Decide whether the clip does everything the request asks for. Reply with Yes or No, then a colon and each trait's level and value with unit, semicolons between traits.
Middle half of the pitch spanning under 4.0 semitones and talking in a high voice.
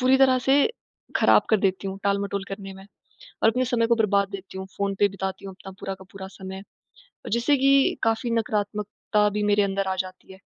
Yes: narrow, 2.6 semitones; high, 200 Hz